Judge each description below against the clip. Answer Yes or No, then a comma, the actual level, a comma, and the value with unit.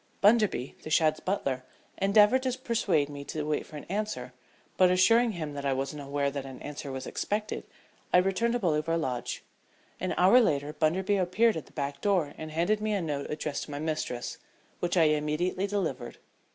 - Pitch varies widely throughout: Yes, wide, 5.8 semitones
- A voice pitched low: No, medium, 160 Hz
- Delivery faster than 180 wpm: Yes, average, 190 wpm